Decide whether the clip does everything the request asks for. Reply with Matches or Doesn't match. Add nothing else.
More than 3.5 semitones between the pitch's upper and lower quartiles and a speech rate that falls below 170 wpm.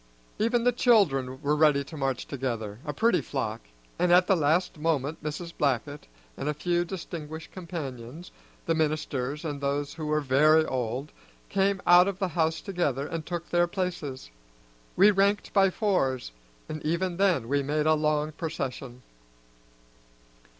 Matches